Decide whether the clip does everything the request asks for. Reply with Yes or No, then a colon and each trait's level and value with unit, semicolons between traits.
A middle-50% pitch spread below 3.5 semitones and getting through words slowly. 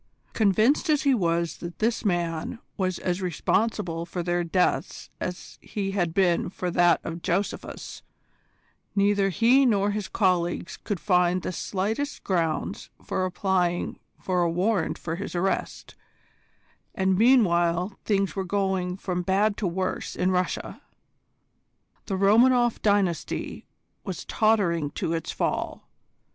Yes: average, 2.7 semitones; slow, 130 wpm